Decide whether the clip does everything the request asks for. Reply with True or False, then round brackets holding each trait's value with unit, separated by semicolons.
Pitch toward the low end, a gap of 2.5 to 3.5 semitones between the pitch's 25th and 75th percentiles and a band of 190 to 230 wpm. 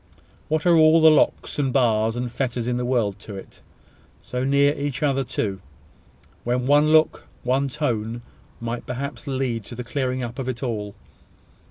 False (125 Hz; 3.1 semitones; 175 wpm)